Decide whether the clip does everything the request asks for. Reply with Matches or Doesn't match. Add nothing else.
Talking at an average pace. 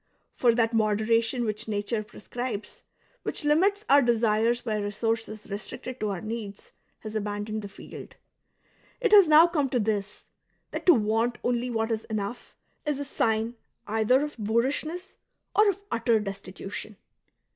Matches